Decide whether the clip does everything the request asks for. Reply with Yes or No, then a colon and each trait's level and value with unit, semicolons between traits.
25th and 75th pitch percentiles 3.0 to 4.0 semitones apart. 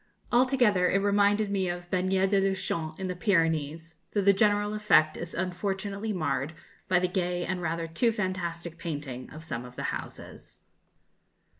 Yes: average, 3.4 semitones